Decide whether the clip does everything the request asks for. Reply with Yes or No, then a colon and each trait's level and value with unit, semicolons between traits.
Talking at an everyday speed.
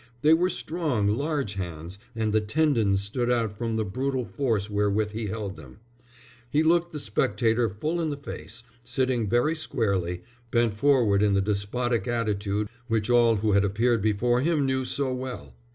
Yes: average, 170 wpm